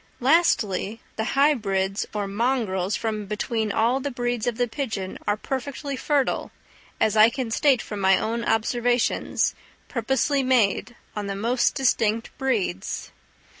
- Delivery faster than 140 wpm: No, slow, 135 wpm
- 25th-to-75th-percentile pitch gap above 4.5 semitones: No, average, 3.8 semitones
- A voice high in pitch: Yes, high, 230 Hz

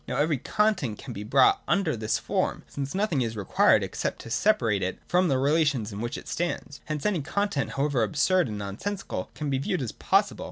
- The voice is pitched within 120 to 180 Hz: Yes, medium, 140 Hz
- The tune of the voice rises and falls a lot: Yes, wide, 7.4 semitones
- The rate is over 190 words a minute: Yes, fast, 205 wpm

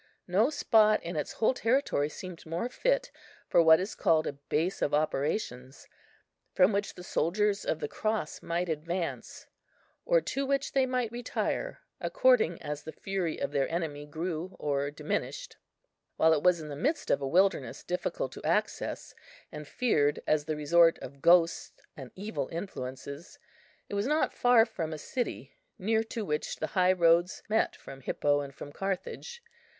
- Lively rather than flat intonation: Yes, wide, 6.5 semitones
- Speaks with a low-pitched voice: No, medium, 175 Hz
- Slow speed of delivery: No, average, 165 wpm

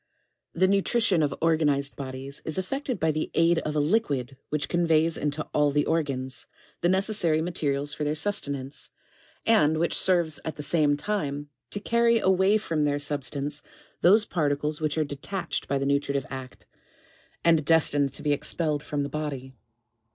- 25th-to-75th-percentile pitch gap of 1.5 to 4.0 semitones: Yes, average, 3.3 semitones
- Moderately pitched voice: Yes, medium, 150 Hz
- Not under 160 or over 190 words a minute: Yes, average, 175 wpm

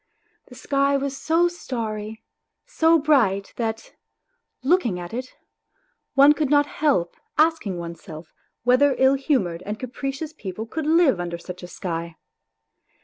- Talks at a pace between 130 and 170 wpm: Yes, slow, 135 wpm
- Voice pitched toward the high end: Yes, very high, 255 Hz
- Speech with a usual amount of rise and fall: No, wide, 7.6 semitones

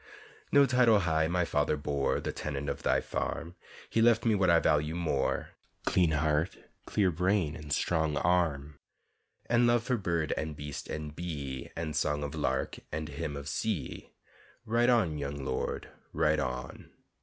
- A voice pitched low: Yes, very low, 80 Hz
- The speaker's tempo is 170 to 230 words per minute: No, average, 160 wpm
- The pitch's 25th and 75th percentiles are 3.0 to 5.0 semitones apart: Yes, average, 3.9 semitones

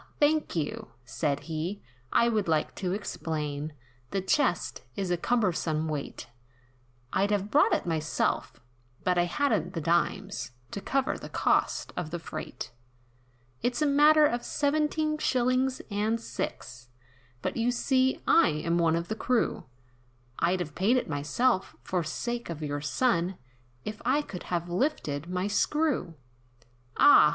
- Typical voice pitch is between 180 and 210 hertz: Yes, medium, 185 Hz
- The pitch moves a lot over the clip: Yes, wide, 7.8 semitones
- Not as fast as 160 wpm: Yes, average, 145 wpm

